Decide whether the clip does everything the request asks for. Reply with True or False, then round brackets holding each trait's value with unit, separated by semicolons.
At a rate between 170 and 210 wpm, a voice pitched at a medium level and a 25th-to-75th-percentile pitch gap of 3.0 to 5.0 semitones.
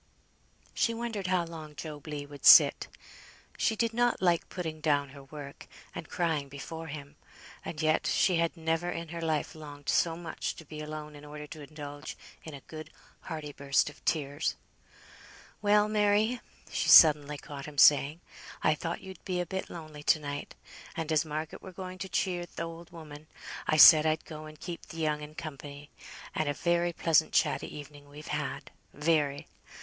False (180 wpm; 155 Hz; 2.5 semitones)